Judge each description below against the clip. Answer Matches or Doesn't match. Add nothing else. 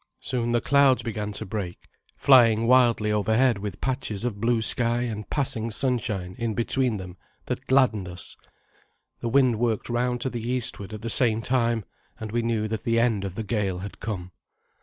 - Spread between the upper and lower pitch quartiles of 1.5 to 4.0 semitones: Matches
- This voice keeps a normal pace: Matches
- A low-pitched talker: Matches